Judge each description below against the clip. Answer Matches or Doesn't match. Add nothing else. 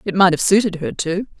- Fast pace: Matches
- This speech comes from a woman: Matches